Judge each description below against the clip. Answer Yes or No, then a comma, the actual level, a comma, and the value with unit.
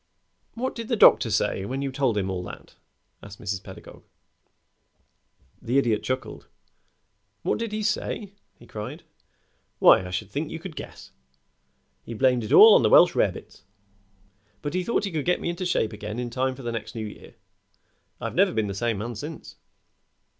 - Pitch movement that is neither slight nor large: No, wide, 7.5 semitones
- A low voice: Yes, low, 125 Hz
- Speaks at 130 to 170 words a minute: No, average, 180 wpm